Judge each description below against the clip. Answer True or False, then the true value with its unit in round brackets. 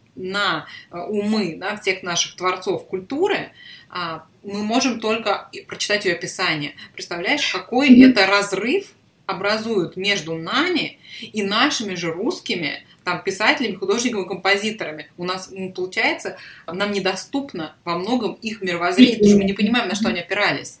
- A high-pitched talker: True (200 Hz)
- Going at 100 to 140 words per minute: True (135 wpm)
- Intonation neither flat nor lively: True (3.3 semitones)